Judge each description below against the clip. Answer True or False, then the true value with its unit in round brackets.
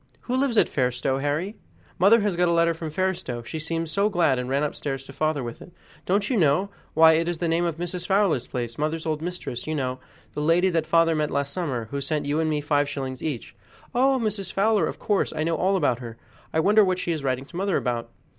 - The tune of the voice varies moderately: True (4.6 semitones)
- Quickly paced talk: True (240 wpm)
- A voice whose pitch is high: False (160 Hz)